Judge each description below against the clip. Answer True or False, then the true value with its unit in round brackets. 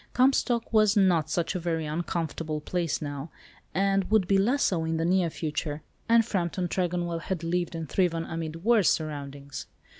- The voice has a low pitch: False (170 Hz)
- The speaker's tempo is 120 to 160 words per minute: False (170 wpm)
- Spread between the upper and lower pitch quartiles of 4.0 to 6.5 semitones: False (3.3 semitones)